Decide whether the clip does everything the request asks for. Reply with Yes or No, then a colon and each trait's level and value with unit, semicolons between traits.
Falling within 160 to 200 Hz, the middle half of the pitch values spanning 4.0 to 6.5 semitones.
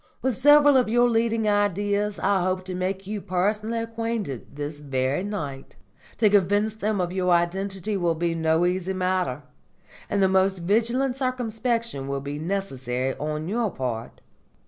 Yes: high, 190 Hz; average, 4.7 semitones